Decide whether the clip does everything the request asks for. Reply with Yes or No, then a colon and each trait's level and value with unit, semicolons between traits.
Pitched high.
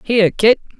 Yes: high, 210 Hz